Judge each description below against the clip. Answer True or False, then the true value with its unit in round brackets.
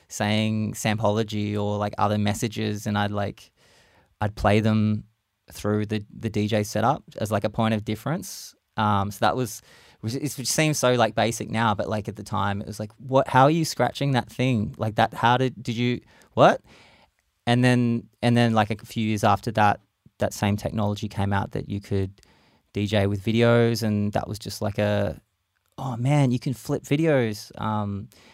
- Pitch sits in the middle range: False (110 Hz)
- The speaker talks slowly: False (190 wpm)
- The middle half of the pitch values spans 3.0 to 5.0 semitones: False (2.4 semitones)